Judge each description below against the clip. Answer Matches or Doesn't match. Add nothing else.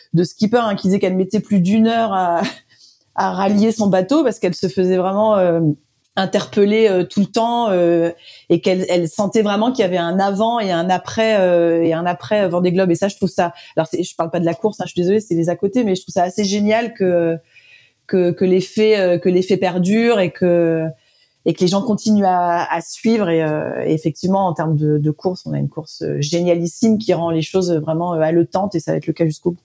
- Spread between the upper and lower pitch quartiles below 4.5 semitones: Matches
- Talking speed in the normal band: Doesn't match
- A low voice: Doesn't match